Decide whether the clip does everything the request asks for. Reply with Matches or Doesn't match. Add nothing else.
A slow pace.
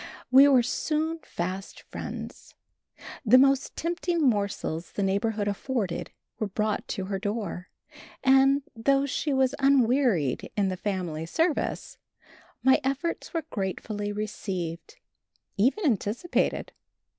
Matches